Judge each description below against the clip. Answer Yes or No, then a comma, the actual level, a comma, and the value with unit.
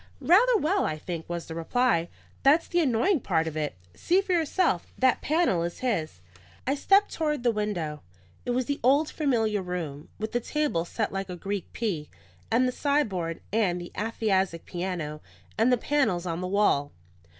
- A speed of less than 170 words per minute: No, average, 180 wpm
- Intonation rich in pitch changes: Yes, wide, 8.5 semitones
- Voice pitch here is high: Yes, high, 215 Hz